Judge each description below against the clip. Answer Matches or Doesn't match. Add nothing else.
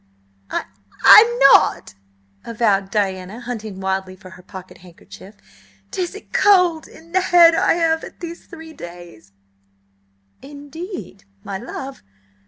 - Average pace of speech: Doesn't match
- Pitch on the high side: Matches